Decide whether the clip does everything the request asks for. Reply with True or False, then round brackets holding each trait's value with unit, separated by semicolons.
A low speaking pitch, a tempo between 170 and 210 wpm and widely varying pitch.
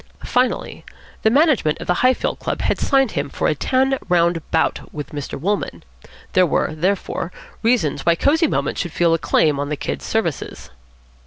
False (180 Hz; 175 wpm; 8.0 semitones)